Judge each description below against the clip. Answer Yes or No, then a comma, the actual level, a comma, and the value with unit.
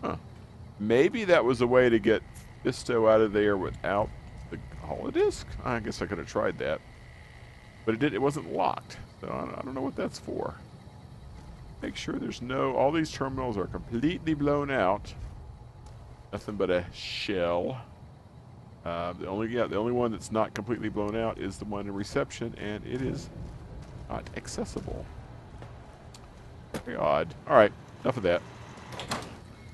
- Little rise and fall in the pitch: No, average, 3.2 semitones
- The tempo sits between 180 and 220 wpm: No, average, 155 wpm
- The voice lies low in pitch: Yes, low, 110 Hz